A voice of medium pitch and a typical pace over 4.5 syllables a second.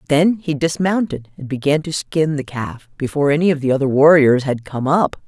Yes: medium, 145 Hz; 5.3 syllables/s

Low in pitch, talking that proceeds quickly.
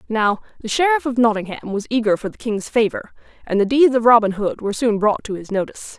No: high, 225 Hz; fast, 230 wpm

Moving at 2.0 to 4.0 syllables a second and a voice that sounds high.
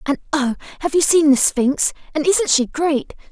No: 4.6 syllables/s; very high, 295 Hz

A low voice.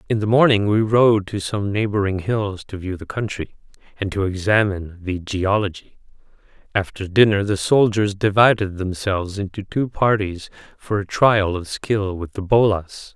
Yes: low, 100 Hz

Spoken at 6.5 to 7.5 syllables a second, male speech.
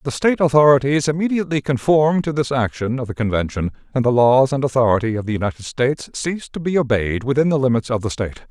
Yes: 6.8 syllables/s; male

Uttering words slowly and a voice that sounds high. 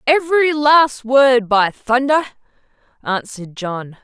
Yes: slow, 105 wpm; very high, 255 Hz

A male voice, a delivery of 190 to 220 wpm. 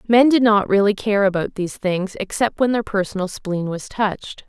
No: female; average, 200 wpm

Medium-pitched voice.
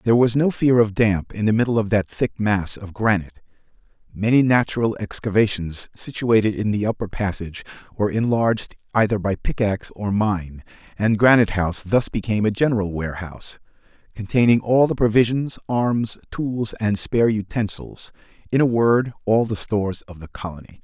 No: low, 105 Hz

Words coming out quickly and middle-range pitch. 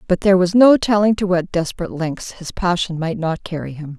Yes: fast, 225 wpm; medium, 180 Hz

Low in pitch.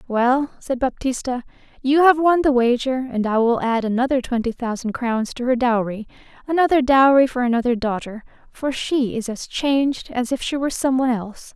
No: very high, 250 Hz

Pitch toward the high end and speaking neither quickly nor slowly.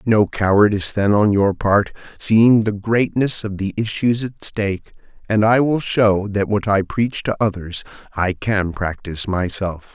No: low, 105 Hz; average, 170 wpm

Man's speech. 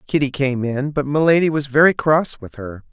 Yes: male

